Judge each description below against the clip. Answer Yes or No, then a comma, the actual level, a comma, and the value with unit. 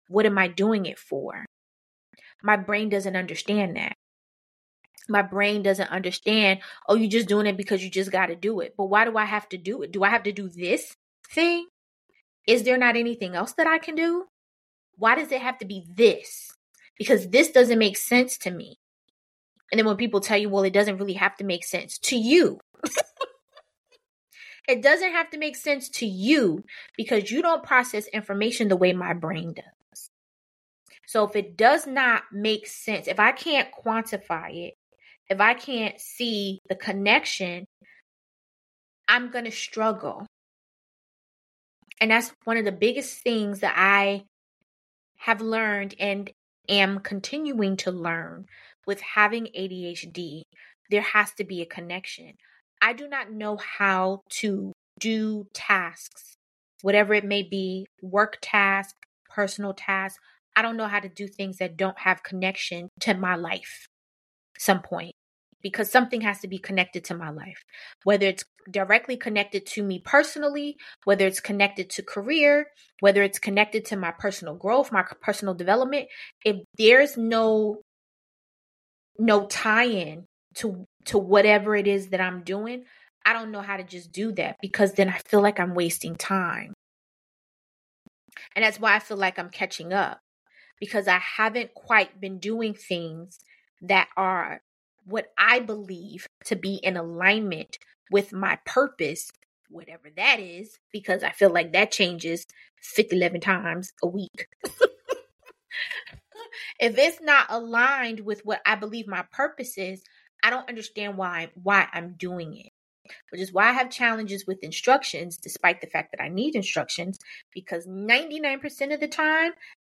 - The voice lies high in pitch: Yes, high, 205 Hz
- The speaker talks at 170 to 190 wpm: No, average, 160 wpm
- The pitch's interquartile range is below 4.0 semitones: Yes, average, 3.5 semitones